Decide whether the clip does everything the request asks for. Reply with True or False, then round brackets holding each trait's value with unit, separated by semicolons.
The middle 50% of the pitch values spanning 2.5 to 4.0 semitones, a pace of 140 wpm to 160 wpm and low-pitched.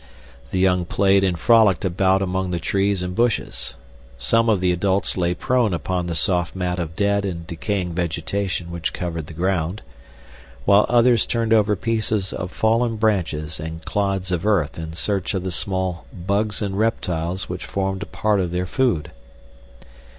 False (2.9 semitones; 170 wpm; 95 Hz)